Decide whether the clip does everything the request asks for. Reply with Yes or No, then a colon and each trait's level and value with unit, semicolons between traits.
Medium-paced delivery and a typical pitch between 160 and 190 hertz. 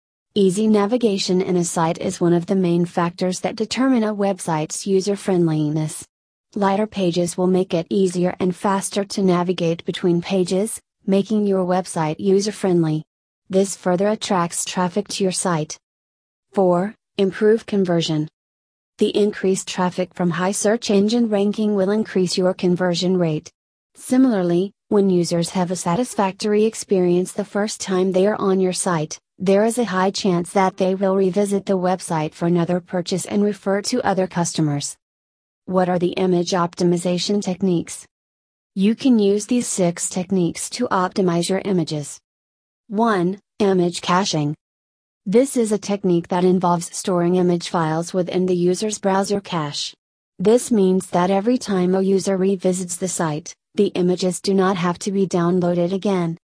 Yes: average, 150 wpm; medium, 185 Hz